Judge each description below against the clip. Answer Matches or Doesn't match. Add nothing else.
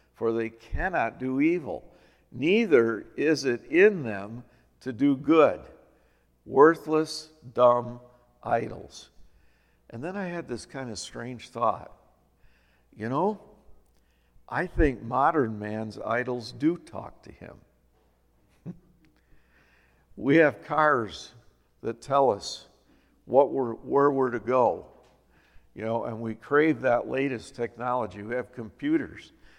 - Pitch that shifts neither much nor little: Doesn't match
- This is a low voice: Matches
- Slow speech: Matches